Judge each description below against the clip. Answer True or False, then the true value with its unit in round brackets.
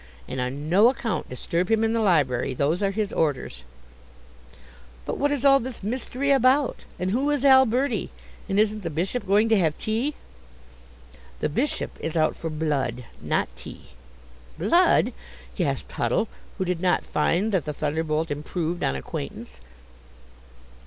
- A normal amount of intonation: False (7.1 semitones)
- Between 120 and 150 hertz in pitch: False (185 Hz)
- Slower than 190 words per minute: True (150 wpm)